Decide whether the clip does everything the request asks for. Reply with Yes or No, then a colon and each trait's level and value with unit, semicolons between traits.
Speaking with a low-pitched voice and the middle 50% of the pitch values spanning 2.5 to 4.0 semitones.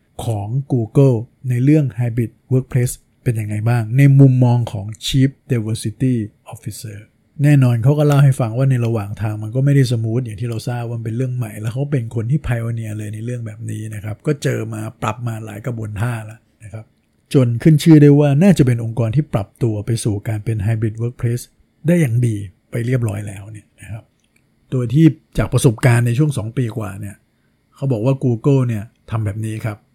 Yes: low, 120 Hz; average, 3.1 semitones